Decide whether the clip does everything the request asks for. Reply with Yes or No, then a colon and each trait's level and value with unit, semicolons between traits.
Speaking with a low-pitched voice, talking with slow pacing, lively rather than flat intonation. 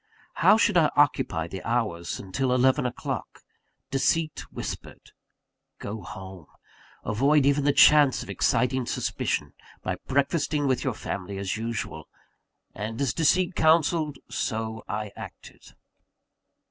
Yes: low, 130 Hz; slow, 120 wpm; wide, 5.7 semitones